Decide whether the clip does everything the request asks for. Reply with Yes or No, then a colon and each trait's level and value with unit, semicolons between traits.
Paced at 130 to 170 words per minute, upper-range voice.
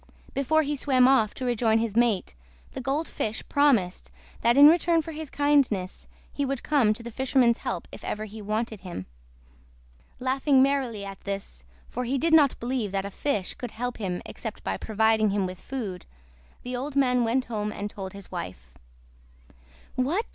No: average, 180 wpm; high, 240 Hz